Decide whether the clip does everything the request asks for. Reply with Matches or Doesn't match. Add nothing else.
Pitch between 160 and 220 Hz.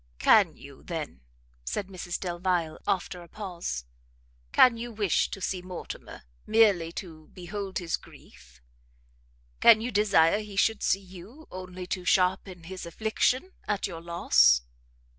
Matches